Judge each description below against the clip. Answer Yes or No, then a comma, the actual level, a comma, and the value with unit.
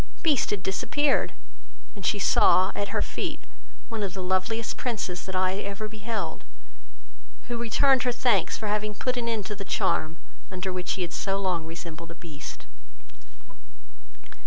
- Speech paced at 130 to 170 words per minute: Yes, average, 160 wpm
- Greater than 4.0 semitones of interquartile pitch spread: No, average, 3.7 semitones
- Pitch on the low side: No, high, 200 Hz